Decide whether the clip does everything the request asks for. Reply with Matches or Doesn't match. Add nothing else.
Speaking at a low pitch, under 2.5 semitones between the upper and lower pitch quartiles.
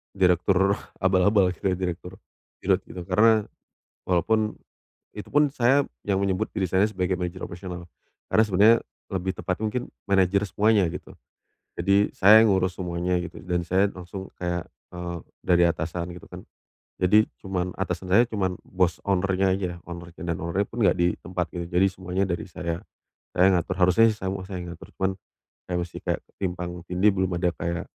Matches